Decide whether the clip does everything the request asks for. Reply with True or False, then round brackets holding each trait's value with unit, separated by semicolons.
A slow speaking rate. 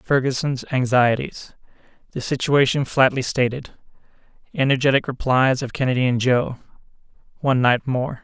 True (85 wpm)